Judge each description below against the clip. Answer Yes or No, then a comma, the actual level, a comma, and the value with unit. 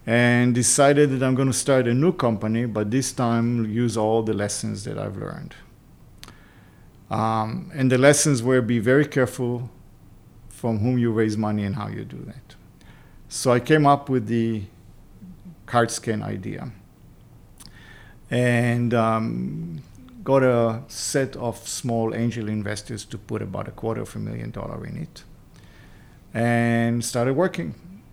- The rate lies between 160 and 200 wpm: No, average, 150 wpm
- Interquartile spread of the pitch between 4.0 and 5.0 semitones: No, average, 2.7 semitones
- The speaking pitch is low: Yes, low, 115 Hz